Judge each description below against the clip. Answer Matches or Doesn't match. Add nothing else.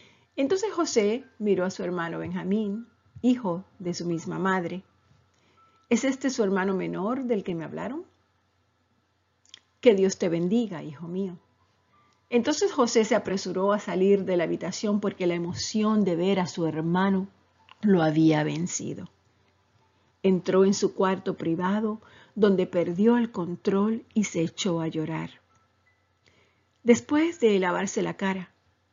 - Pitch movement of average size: Matches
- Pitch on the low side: Doesn't match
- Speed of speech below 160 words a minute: Matches